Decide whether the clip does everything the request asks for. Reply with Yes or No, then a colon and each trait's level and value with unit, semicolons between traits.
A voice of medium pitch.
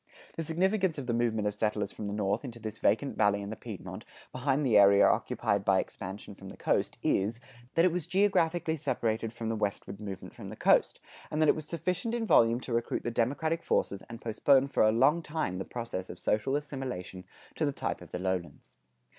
No: low, 115 Hz